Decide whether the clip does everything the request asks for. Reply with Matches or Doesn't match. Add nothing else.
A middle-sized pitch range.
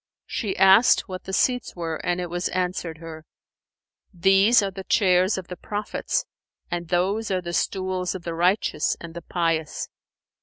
Doesn't match